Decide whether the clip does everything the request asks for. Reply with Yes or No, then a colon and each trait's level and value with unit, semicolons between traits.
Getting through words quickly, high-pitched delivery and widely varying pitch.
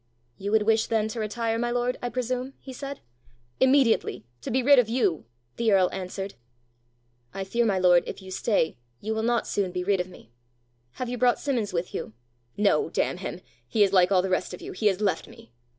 No: fast, 215 wpm; high, 220 Hz; average, 4.3 semitones